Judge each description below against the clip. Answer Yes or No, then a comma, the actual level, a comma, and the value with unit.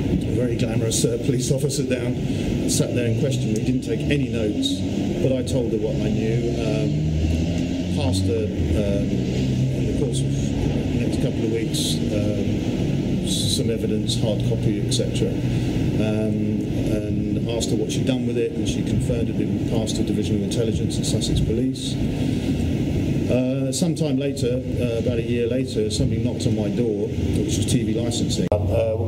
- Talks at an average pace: Yes, average, 170 wpm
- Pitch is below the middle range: Yes, low, 115 Hz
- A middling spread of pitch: Yes, average, 3.6 semitones